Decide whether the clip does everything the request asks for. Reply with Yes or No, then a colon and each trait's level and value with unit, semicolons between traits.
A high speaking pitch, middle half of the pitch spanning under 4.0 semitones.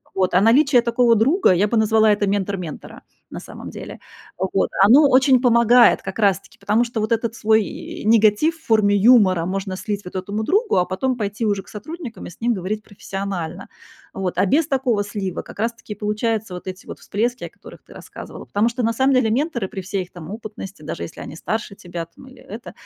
Yes: high, 215 Hz; average, 3.5 semitones